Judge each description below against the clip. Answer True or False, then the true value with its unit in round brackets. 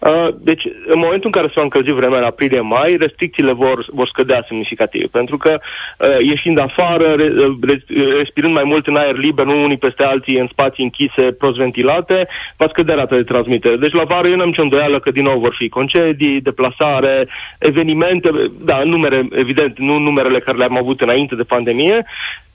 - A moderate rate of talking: False (175 wpm)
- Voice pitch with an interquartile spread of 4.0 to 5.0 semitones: False (3.6 semitones)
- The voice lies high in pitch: False (140 Hz)